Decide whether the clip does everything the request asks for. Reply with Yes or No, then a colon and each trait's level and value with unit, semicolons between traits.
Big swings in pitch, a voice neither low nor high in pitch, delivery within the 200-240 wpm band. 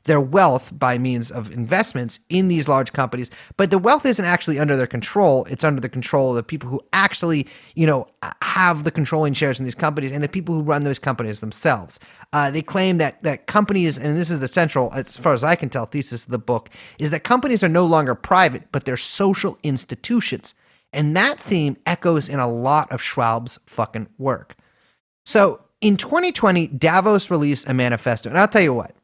Yes: wide, 5.7 semitones; medium, 145 Hz; fast, 205 wpm